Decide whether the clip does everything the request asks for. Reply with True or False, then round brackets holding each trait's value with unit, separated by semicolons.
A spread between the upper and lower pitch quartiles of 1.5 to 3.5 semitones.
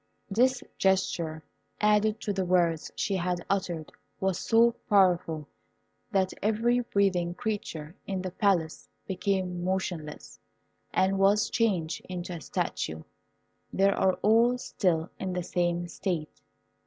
True (2.8 semitones)